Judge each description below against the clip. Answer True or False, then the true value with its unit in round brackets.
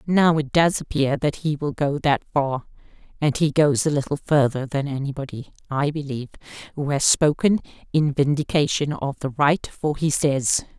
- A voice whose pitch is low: False (145 Hz)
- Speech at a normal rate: True (170 wpm)